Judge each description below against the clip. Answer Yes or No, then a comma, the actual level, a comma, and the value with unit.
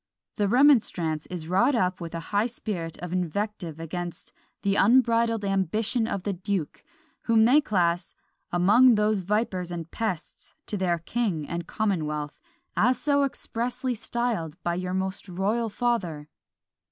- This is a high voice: Yes, high, 200 Hz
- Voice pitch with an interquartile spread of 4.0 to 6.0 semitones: Yes, average, 4.9 semitones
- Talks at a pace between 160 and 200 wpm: No, average, 140 wpm